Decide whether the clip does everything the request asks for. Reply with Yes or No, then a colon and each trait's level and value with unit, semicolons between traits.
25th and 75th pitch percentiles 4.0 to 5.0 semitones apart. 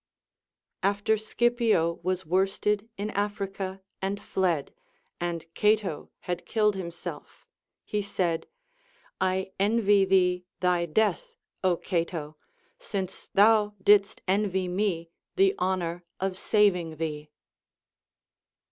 No: average, 2.8 semitones